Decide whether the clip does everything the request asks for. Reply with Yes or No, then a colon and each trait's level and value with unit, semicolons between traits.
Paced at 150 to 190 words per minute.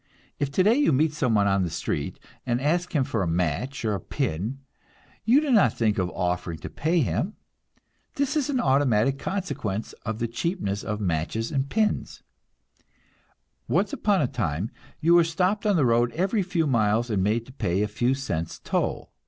Yes: average, 185 wpm